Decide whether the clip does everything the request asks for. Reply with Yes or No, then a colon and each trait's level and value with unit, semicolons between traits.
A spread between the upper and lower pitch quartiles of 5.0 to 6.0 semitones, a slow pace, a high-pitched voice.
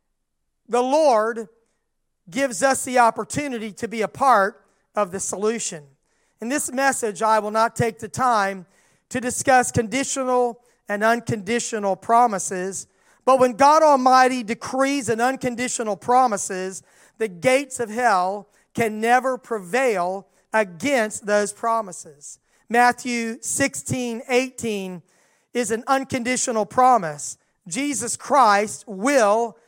No: average, 3.7 semitones; slow, 110 wpm; high, 230 Hz